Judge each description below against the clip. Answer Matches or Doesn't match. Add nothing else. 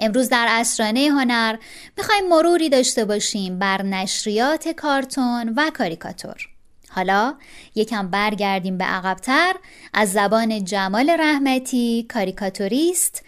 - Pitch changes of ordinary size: Doesn't match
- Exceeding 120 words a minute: Doesn't match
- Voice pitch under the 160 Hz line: Doesn't match